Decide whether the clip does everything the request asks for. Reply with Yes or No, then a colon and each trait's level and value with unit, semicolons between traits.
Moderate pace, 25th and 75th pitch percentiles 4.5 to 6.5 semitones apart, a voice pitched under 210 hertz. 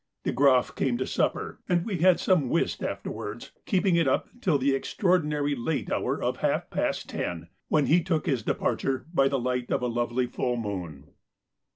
Yes: average, 185 wpm; wide, 5.6 semitones; low, 135 Hz